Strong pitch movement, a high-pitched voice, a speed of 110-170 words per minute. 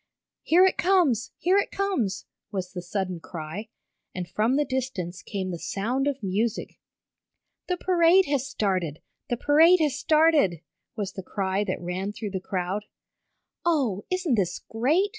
Yes: wide, 8.4 semitones; high, 220 Hz; average, 155 wpm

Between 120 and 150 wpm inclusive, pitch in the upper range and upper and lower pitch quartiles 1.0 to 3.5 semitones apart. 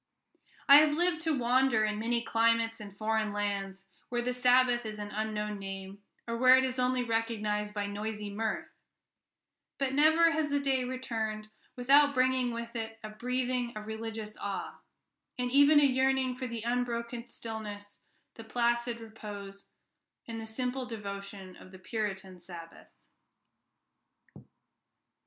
Yes: average, 145 wpm; high, 230 Hz; average, 3.2 semitones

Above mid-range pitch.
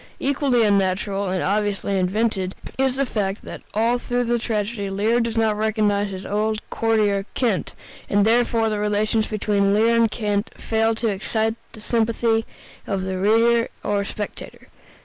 Yes: high, 215 Hz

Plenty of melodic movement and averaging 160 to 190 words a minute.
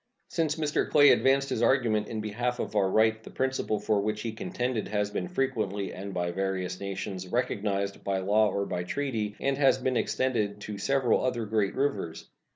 No: average, 4.5 semitones; average, 185 wpm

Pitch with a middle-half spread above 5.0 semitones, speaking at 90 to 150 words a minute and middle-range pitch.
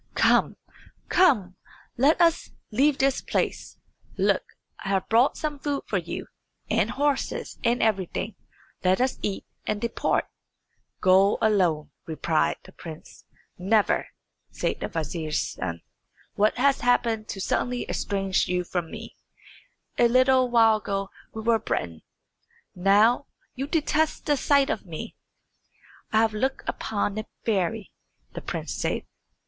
No: wide, 5.4 semitones; slow, 135 wpm; high, 220 Hz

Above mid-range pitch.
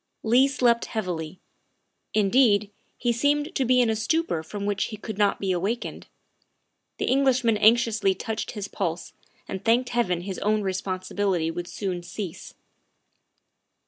Yes: high, 210 Hz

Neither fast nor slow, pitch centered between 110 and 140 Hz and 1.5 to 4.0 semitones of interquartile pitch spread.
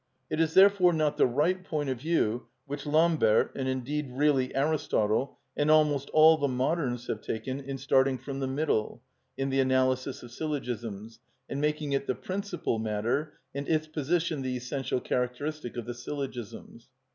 Yes: average, 165 wpm; low, 135 Hz; average, 3.5 semitones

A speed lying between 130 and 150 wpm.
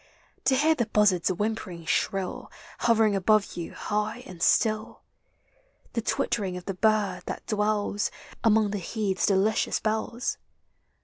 Yes: slow, 135 wpm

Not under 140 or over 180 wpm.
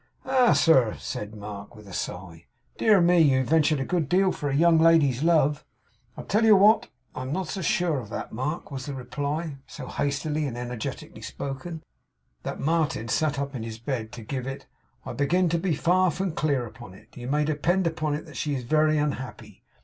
No: average, 200 wpm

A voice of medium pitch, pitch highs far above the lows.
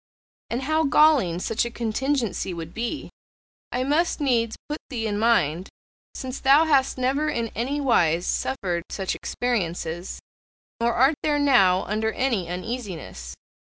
No: high, 235 Hz; wide, 6.5 semitones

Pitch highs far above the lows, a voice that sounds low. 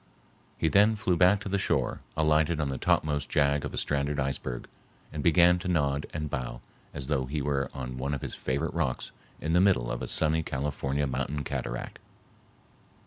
No: average, 3.2 semitones; very low, 75 Hz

